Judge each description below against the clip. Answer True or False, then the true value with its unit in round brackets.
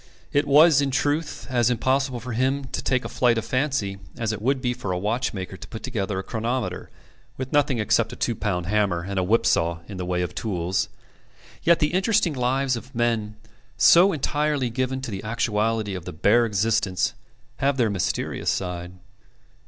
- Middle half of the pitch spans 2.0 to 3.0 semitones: False (4.8 semitones)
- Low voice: True (115 Hz)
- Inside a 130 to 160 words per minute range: False (190 wpm)